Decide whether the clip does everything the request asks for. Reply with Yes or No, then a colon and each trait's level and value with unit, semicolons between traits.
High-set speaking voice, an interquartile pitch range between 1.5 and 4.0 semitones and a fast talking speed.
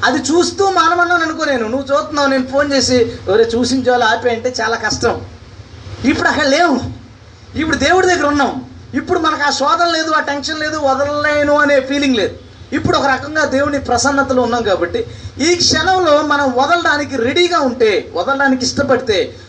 Yes: very high, 285 Hz; average, 3.7 semitones; fast, 150 wpm